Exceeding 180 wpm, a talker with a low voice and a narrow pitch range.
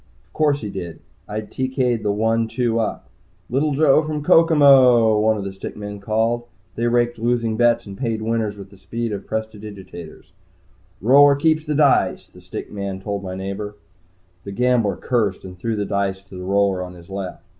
No: average, 190 wpm; low, 110 Hz; average, 3.7 semitones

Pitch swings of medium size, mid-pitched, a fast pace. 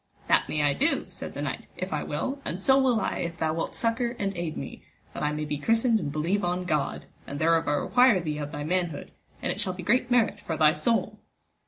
No: wide, 6.9 semitones; medium, 175 Hz; fast, 240 wpm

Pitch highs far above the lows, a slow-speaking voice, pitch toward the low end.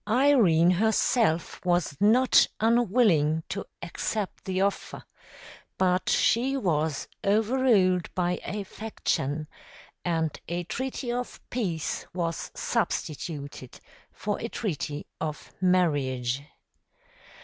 No: wide, 5.7 semitones; slow, 95 wpm; medium, 185 Hz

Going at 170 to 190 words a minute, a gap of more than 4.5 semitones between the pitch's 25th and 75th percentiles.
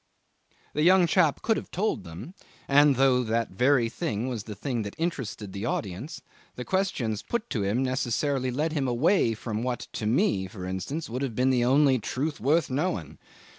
Yes: average, 185 wpm; average, 5.2 semitones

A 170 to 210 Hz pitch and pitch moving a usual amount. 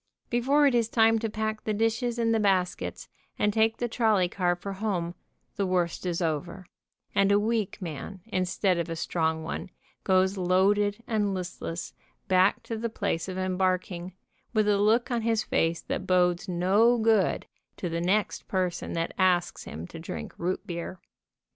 Yes: high, 190 Hz; average, 3.6 semitones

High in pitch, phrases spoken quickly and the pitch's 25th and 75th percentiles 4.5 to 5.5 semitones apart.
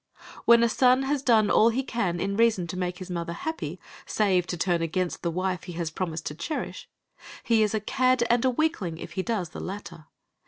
Yes: high, 195 Hz; fast, 220 wpm; average, 5.2 semitones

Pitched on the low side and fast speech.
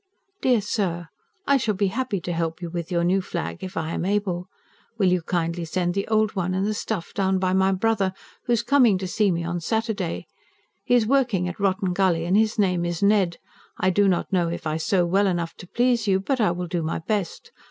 No: high, 190 Hz; fast, 230 wpm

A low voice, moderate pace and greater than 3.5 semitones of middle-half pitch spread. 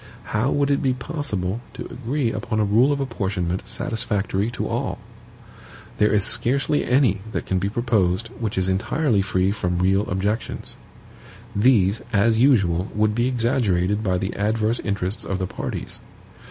Yes: low, 105 Hz; average, 155 wpm; average, 4.0 semitones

